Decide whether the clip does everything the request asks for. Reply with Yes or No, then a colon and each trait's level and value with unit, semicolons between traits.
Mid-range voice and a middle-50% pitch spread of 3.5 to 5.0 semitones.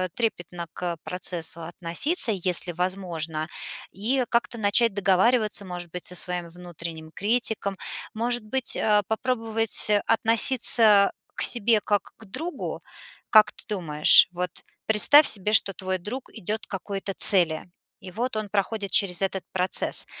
No: high, 200 Hz; average, 3.9 semitones